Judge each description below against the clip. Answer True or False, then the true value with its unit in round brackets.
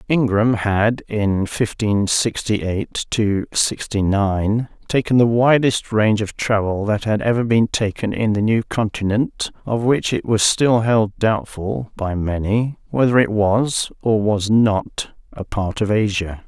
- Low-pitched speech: True (110 Hz)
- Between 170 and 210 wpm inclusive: False (155 wpm)